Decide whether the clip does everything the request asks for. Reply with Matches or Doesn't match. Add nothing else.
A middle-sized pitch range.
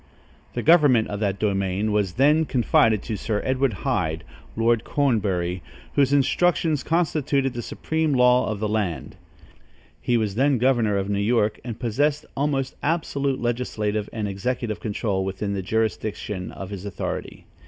Matches